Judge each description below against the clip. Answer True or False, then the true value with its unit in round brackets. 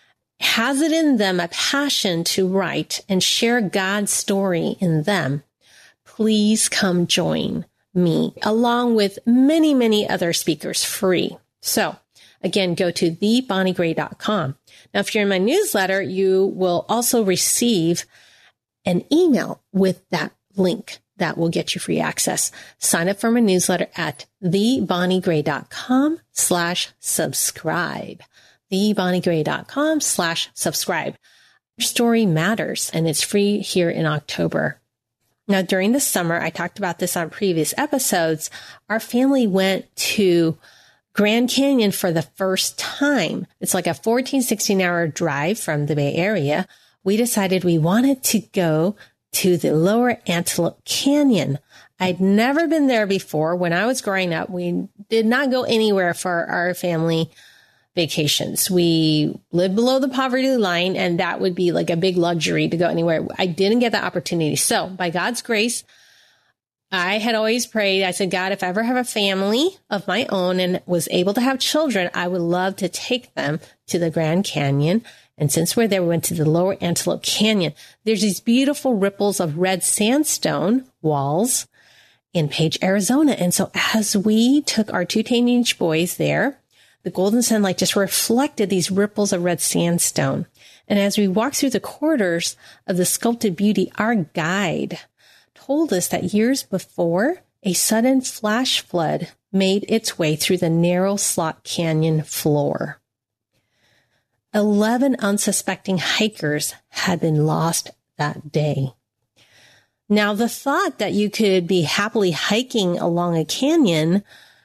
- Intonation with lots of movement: False (4.5 semitones)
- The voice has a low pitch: False (190 Hz)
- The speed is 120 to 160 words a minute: True (150 wpm)